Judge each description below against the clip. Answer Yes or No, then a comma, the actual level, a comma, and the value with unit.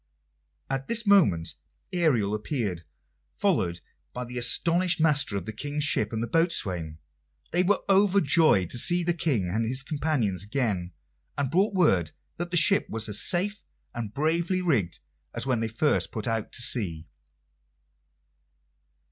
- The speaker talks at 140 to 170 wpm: Yes, average, 150 wpm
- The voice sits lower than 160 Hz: Yes, low, 135 Hz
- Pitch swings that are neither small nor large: No, wide, 8.4 semitones